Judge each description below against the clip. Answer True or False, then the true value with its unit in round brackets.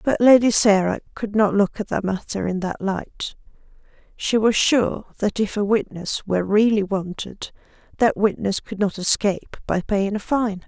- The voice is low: False (205 Hz)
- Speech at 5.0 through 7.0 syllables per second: False (4.6 syllables/s)